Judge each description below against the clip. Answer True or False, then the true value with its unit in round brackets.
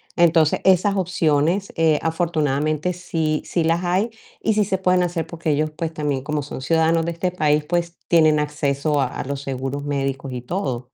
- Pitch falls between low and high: True (160 Hz)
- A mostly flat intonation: False (3.1 semitones)